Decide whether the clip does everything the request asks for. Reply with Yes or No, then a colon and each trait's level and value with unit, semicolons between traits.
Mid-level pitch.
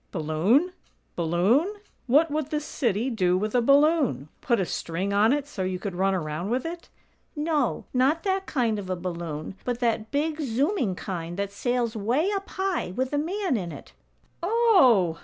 No: high, 240 Hz